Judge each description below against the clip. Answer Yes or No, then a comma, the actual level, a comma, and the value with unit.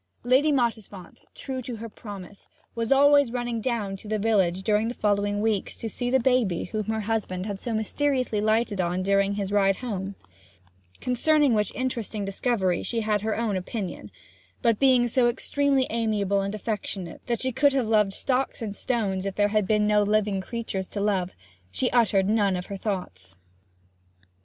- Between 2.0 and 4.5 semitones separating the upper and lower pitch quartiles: Yes, average, 3.4 semitones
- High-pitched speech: Yes, high, 215 Hz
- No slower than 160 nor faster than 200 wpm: Yes, average, 175 wpm